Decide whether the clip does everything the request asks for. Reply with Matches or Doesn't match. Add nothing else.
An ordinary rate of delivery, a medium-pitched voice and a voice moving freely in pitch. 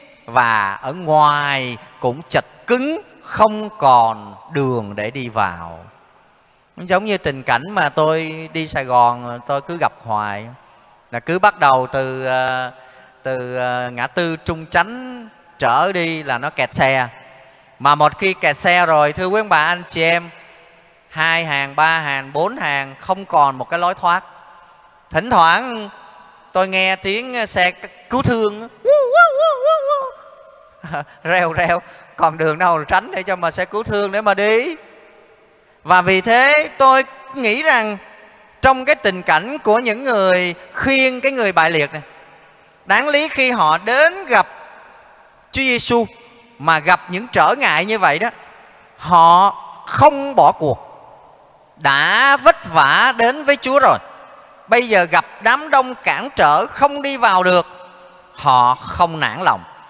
Doesn't match